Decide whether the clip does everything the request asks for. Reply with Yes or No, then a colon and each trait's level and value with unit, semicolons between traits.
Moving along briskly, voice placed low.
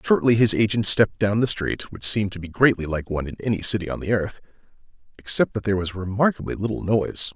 Yes: fast, 220 wpm; low, 105 Hz